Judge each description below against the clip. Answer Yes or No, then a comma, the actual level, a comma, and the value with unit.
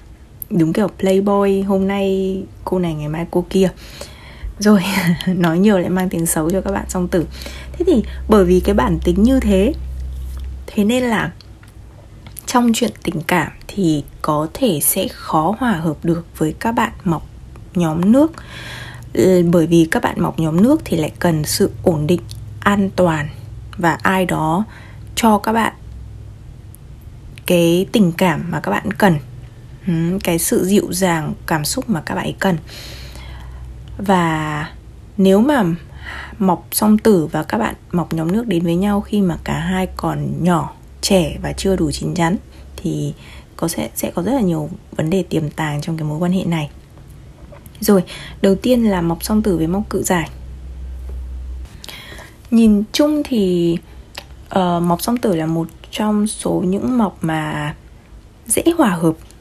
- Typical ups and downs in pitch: Yes, average, 4.2 semitones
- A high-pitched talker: No, medium, 180 Hz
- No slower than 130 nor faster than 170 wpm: Yes, slow, 165 wpm